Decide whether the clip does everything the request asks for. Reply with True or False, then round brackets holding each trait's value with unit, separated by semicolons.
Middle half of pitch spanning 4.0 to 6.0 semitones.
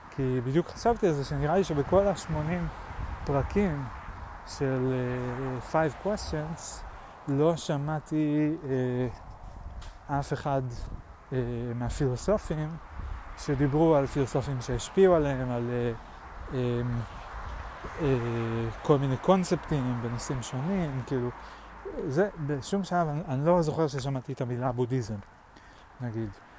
True (4.3 semitones)